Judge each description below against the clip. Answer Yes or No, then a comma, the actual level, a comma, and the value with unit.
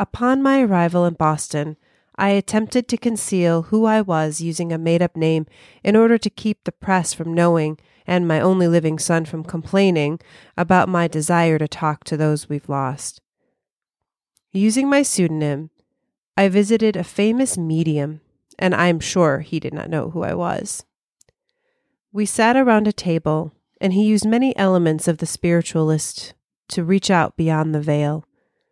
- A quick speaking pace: No, average, 165 wpm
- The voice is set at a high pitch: No, medium, 170 Hz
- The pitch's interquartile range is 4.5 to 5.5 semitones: Yes, average, 5.0 semitones